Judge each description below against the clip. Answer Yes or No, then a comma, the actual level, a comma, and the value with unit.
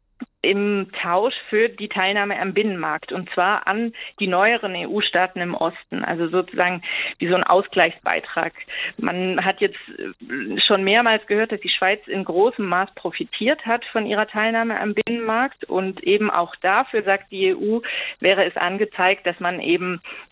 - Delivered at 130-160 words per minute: Yes, average, 155 wpm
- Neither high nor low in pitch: No, high, 200 Hz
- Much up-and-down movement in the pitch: No, average, 3.0 semitones